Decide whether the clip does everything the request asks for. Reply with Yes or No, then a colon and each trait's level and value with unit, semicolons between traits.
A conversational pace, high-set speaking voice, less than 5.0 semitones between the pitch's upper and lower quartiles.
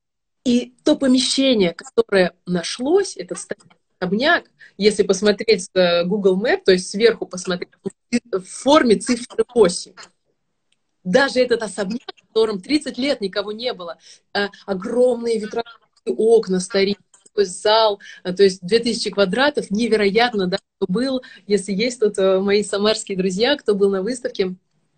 Yes: average, 125 wpm; high, 210 Hz; average, 3.6 semitones